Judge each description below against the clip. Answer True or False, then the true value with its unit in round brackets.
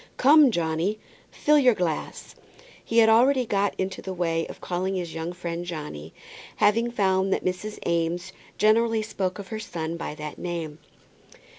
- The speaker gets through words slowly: False (160 wpm)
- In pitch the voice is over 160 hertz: True (185 Hz)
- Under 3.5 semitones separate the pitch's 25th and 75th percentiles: False (4.6 semitones)